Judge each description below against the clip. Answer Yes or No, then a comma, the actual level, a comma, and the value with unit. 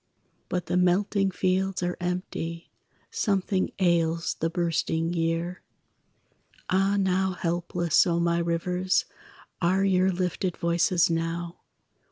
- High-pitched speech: No, medium, 175 Hz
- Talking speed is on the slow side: Yes, slow, 110 wpm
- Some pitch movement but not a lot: No, narrow, 1.7 semitones